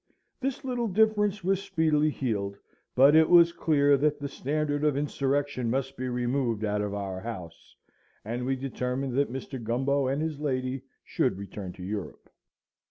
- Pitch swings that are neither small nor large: Yes, average, 4.1 semitones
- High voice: No, low, 135 Hz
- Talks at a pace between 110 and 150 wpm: No, average, 165 wpm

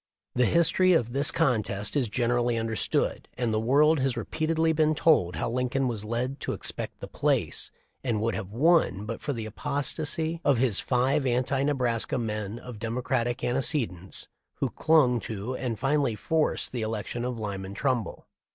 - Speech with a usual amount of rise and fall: Yes, average, 4.0 semitones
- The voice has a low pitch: Yes, low, 125 Hz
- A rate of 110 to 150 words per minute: No, average, 165 wpm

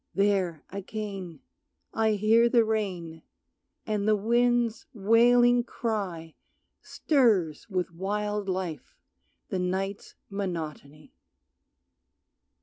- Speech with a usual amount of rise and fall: Yes, average, 3.6 semitones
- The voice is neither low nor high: No, high, 200 Hz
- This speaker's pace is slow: Yes, slow, 85 wpm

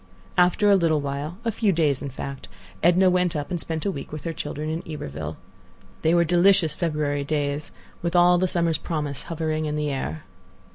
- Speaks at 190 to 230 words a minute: Yes, average, 195 wpm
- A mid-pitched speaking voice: Yes, medium, 155 Hz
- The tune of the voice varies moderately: Yes, average, 3.2 semitones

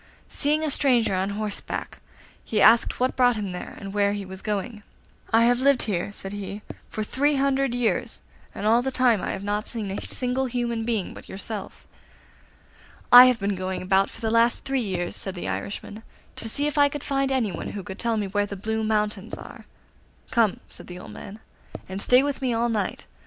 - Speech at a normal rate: No, fast, 210 wpm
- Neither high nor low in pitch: No, high, 220 Hz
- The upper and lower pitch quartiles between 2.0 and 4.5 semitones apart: Yes, average, 3.7 semitones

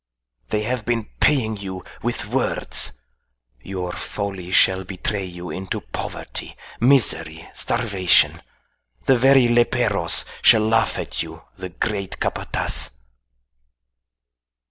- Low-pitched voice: Yes, low, 105 Hz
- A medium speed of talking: No, slow, 105 wpm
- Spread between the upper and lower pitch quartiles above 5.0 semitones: No, average, 4.1 semitones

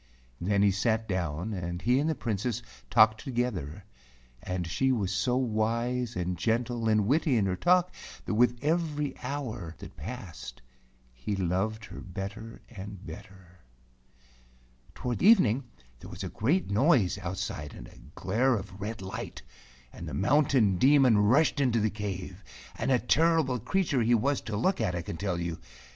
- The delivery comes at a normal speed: Yes, average, 165 wpm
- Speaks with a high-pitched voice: No, low, 110 Hz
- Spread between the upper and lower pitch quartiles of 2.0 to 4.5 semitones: No, average, 5.0 semitones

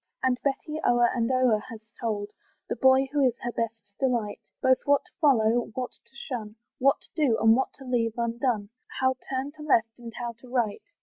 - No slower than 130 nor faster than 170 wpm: No, average, 195 wpm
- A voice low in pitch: No, high, 245 Hz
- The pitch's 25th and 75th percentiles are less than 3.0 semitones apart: Yes, narrow, 2.6 semitones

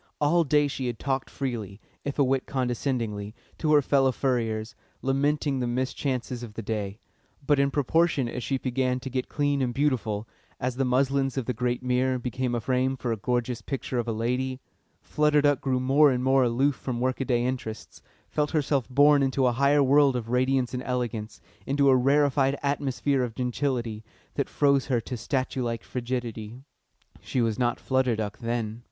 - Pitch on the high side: No, low, 130 Hz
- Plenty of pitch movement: No, narrow, 2.4 semitones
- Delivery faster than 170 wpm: Yes, average, 185 wpm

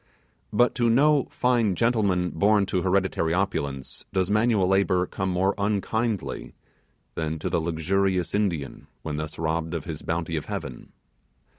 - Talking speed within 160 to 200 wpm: No, average, 150 wpm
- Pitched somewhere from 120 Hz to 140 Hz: No, very low, 95 Hz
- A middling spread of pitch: Yes, average, 4.1 semitones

